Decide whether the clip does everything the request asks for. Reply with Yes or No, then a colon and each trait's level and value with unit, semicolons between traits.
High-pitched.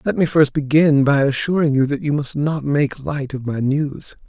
No: medium, 145 Hz